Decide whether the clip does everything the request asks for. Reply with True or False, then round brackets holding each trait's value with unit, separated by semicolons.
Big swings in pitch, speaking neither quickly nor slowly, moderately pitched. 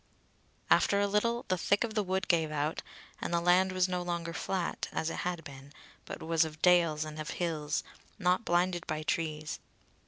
False (3.0 semitones; 190 wpm; 175 Hz)